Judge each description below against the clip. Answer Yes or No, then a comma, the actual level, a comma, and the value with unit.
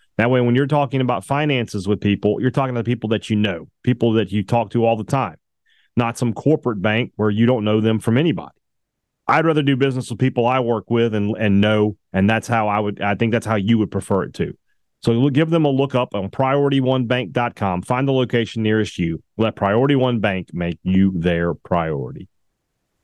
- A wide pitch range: No, average, 3.5 semitones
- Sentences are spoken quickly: Yes, fast, 215 wpm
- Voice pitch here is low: Yes, low, 115 Hz